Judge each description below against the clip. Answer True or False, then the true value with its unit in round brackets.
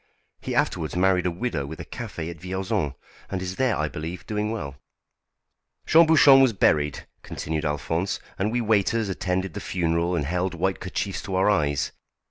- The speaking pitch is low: True (90 Hz)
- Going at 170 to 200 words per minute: True (175 wpm)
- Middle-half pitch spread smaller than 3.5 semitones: False (4.0 semitones)